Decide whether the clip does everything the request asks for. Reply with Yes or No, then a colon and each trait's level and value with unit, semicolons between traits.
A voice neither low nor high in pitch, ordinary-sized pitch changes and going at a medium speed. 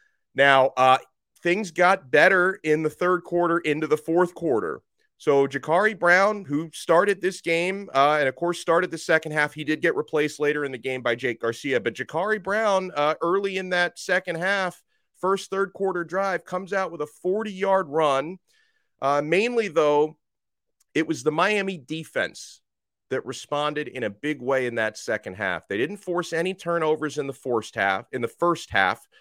Yes: medium, 165 Hz; average, 4.4 semitones; average, 185 wpm